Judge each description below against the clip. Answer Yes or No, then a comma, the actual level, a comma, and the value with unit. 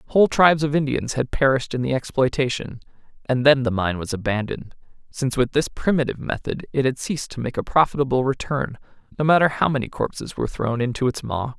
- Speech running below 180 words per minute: No, average, 195 wpm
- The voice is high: No, low, 130 Hz